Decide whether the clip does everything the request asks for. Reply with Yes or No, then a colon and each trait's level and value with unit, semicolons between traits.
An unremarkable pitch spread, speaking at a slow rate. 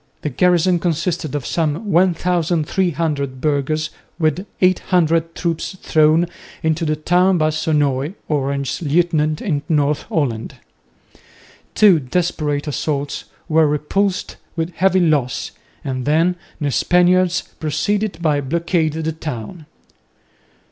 Yes: average, 3.0 semitones; slow, 110 wpm